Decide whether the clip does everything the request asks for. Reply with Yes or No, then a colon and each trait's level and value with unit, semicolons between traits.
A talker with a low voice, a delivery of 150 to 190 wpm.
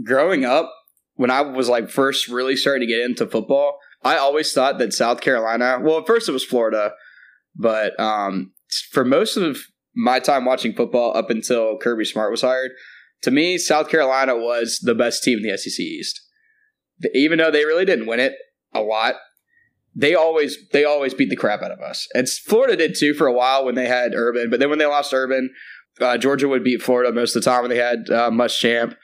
No: low, 130 Hz; fast, 205 wpm